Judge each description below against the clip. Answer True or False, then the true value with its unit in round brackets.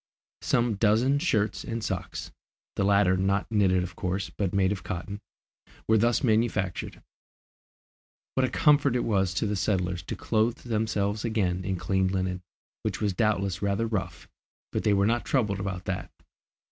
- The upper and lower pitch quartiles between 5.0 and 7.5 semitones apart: False (2.9 semitones)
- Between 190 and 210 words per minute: False (160 wpm)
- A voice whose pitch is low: True (100 Hz)